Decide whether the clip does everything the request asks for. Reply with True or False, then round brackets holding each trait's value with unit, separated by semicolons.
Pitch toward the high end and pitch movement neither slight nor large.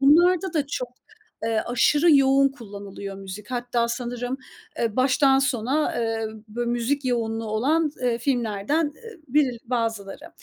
True (245 Hz; 3.8 semitones)